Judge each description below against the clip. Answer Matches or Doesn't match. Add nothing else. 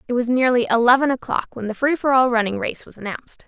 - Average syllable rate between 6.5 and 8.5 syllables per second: Matches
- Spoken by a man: Doesn't match